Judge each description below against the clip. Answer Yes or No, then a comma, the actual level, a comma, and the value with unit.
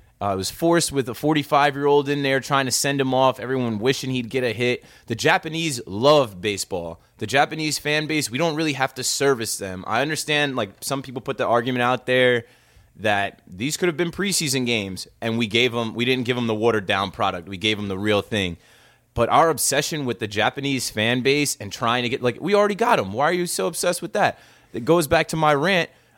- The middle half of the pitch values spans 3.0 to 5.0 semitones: Yes, average, 4.6 semitones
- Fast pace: Yes, fast, 230 wpm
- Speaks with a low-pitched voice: Yes, low, 130 Hz